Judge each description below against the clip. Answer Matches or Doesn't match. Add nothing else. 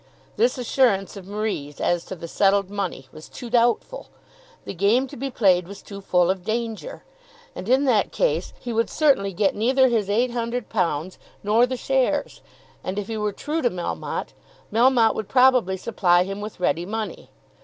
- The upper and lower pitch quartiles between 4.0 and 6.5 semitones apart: Matches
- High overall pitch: Matches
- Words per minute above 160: Matches